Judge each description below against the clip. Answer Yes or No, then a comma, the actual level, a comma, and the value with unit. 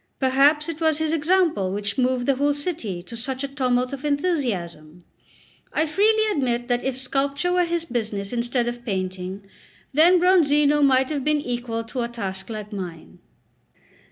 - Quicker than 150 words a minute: Yes, average, 165 wpm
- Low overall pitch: No, very high, 260 Hz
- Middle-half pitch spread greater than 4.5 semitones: Yes, average, 5.2 semitones